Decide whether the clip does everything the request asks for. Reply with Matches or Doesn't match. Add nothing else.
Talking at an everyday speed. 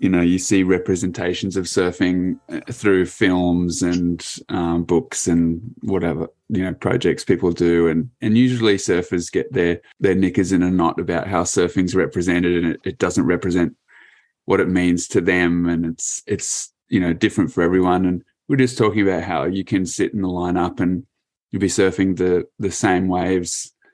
Matches